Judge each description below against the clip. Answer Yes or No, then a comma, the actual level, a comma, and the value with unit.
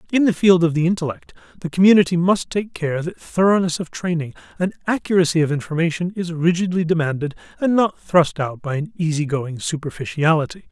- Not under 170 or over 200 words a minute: Yes, average, 175 wpm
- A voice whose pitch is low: No, medium, 170 Hz